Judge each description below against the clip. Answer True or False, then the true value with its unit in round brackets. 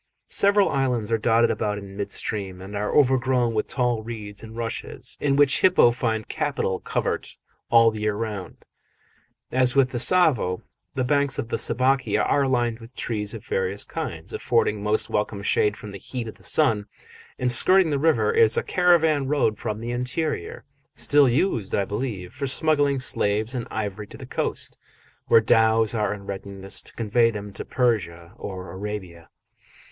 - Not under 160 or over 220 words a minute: True (175 wpm)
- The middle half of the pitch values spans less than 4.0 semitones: False (4.3 semitones)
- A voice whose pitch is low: True (115 Hz)